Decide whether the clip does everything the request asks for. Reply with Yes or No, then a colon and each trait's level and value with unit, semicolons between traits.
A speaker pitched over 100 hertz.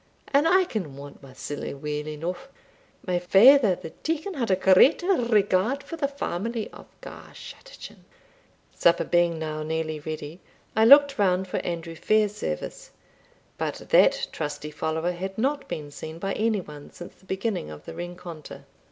Yes: medium, 185 Hz